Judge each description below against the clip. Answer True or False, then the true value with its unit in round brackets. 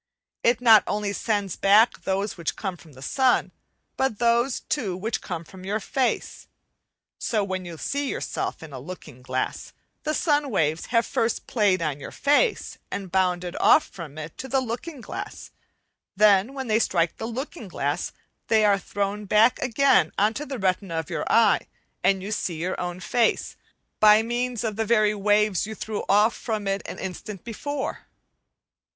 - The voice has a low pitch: False (210 Hz)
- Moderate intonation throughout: True (4.2 semitones)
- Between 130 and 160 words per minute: False (175 wpm)